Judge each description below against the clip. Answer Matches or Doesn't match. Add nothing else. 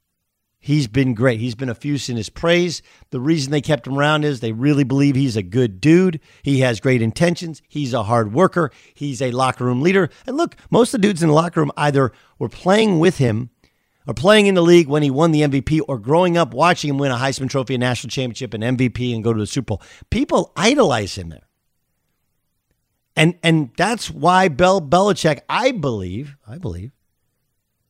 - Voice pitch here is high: Doesn't match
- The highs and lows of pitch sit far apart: Doesn't match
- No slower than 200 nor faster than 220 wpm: Matches